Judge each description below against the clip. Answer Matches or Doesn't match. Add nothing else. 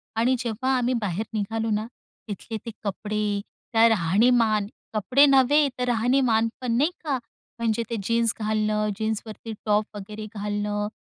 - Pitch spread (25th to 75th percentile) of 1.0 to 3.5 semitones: Matches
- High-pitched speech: Matches